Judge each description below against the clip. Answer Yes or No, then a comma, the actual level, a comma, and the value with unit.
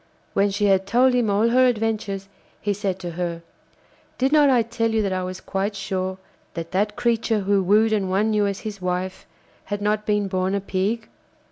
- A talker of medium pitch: No, high, 205 Hz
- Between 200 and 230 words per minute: Yes, fast, 205 wpm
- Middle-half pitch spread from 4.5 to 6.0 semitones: No, narrow, 2.6 semitones